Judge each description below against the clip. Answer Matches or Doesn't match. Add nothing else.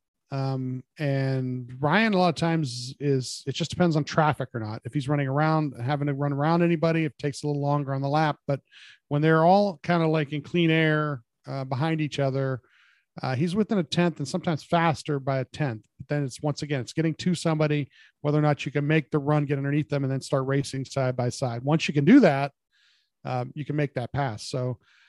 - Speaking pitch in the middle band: Matches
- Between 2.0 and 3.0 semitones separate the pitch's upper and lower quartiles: Matches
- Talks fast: Matches